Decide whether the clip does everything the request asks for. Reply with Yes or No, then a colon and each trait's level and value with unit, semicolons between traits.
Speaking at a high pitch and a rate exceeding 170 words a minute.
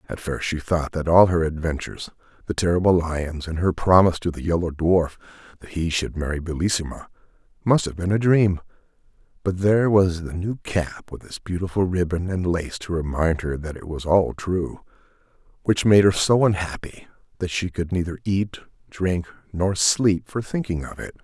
No: very low, 90 Hz; average, 185 wpm